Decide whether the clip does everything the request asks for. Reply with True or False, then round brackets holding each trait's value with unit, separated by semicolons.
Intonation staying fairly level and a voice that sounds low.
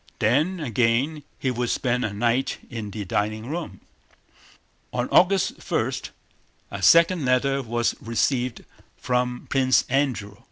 False (3.2 semitones; 125 Hz)